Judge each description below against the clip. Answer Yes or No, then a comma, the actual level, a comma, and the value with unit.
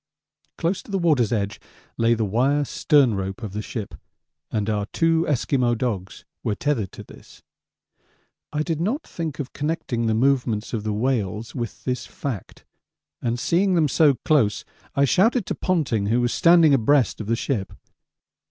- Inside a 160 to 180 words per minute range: Yes, average, 170 wpm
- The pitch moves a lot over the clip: Yes, wide, 5.8 semitones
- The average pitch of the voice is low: Yes, low, 125 Hz